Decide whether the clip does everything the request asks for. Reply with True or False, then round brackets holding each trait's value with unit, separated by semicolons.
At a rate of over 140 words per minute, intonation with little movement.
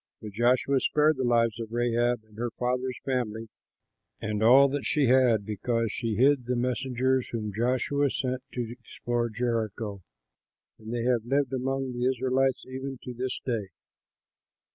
True (155 wpm; 2.1 semitones)